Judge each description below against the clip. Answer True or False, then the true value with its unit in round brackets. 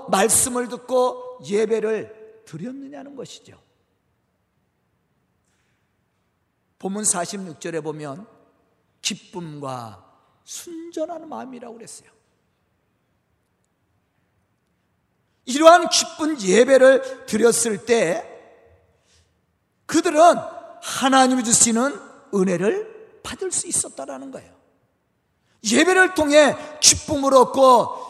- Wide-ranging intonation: True (6.5 semitones)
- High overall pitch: True (250 Hz)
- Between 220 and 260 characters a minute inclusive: False (175 characters per minute)